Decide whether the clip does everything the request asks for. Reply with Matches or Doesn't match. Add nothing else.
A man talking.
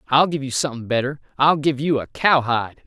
Matches